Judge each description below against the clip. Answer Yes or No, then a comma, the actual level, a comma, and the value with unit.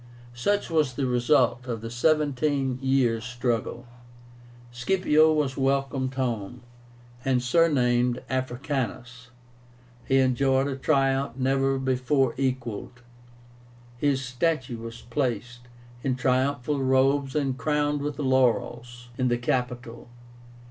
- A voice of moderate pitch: No, low, 130 Hz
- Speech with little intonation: Yes, narrow, 2.1 semitones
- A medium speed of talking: No, slow, 105 wpm